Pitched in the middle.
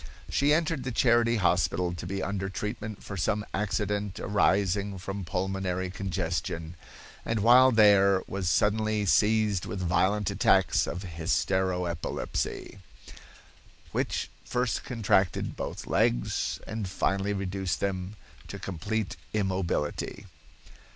No: low, 100 Hz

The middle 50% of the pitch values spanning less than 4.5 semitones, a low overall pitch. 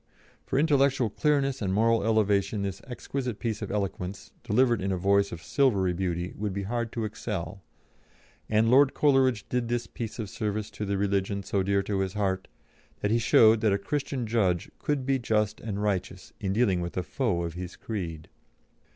Yes: average, 3.6 semitones; low, 105 Hz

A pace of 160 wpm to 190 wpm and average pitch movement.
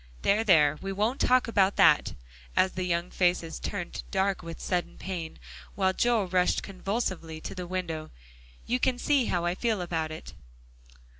Yes: average, 165 wpm; average, 3.0 semitones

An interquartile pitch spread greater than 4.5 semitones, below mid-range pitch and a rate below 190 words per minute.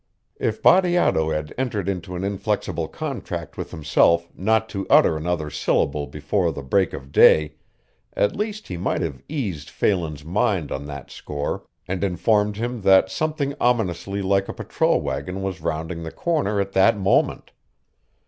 Yes: average, 4.9 semitones; very low, 95 Hz; average, 160 wpm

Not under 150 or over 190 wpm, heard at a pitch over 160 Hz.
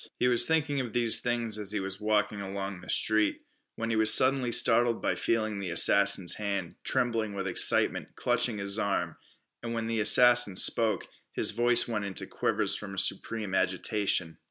No: average, 175 wpm; low, 110 Hz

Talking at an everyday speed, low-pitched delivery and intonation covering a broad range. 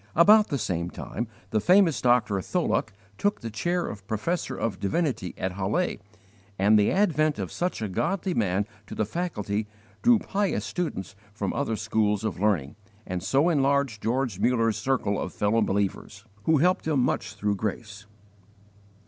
Yes: average, 160 wpm; low, 110 Hz; wide, 7.3 semitones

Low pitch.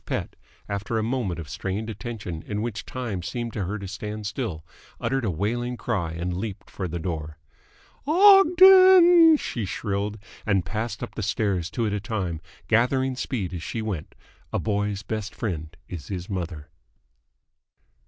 Yes: low, 105 Hz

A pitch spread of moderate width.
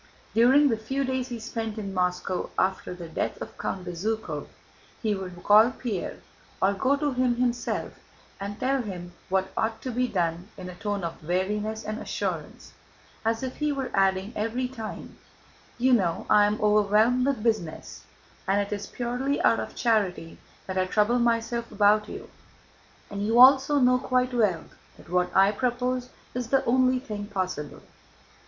Yes: average, 4.4 semitones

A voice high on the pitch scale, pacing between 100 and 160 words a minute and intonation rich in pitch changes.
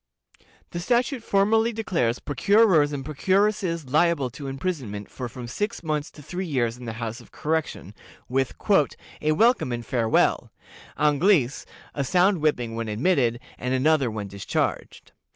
No: medium, 145 Hz; average, 145 wpm; wide, 7.1 semitones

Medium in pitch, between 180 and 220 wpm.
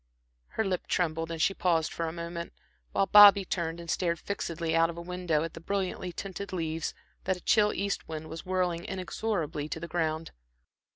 Yes: medium, 170 Hz; average, 190 wpm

